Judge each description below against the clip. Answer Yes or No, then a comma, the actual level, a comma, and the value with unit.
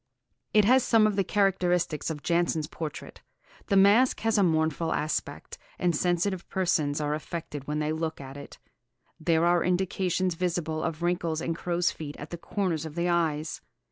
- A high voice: No, medium, 170 Hz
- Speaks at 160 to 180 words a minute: Yes, average, 175 wpm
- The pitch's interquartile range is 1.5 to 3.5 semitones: Yes, average, 2.7 semitones